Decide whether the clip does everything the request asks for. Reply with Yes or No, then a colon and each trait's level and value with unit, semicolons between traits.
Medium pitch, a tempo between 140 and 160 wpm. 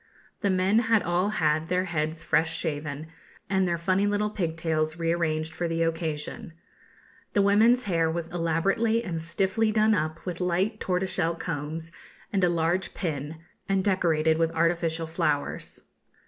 Yes: medium, 170 Hz; average, 145 wpm